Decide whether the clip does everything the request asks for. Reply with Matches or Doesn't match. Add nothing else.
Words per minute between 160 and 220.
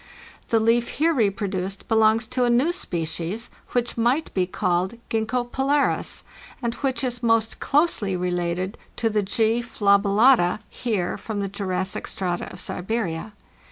Doesn't match